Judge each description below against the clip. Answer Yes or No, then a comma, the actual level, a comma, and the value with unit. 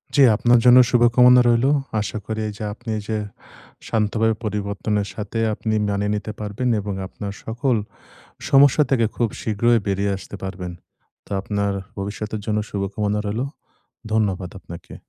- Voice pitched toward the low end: Yes, low, 105 Hz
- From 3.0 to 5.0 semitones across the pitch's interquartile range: No, narrow, 2.6 semitones